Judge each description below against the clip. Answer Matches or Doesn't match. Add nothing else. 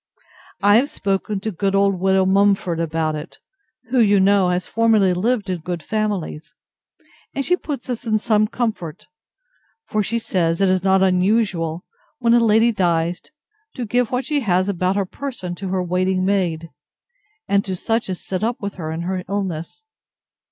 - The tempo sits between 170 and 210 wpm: Matches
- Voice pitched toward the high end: Matches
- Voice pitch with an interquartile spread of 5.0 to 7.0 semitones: Doesn't match